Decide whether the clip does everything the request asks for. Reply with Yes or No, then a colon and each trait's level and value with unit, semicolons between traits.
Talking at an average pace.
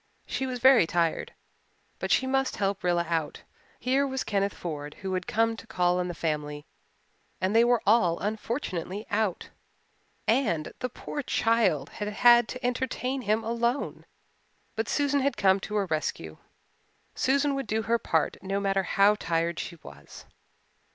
Yes: average, 160 wpm